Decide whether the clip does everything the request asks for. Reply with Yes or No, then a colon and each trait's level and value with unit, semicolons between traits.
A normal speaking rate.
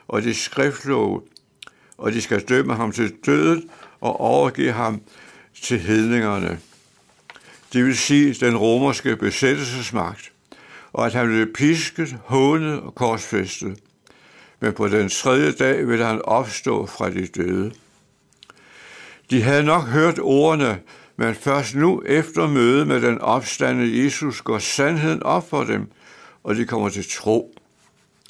No: slow, 135 wpm